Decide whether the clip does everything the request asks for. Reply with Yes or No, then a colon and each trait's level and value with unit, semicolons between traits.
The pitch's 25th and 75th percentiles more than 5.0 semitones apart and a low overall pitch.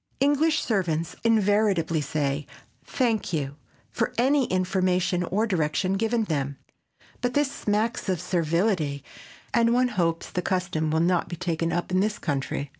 No: wide, 5.4 semitones; medium, 185 Hz